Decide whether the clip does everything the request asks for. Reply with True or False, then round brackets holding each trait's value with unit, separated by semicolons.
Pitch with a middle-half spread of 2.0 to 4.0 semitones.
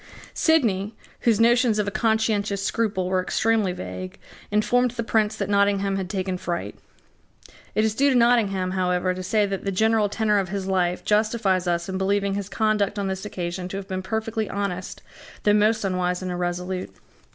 True (2.8 semitones)